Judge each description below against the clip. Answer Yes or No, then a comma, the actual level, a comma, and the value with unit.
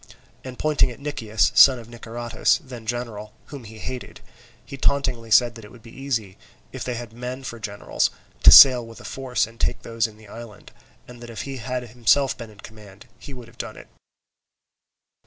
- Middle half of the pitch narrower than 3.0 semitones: Yes, narrow, 2.4 semitones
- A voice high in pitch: No, low, 120 Hz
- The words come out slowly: No, average, 200 wpm